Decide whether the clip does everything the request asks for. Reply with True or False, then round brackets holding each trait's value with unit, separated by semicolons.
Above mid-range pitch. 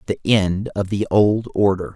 False (100 Hz)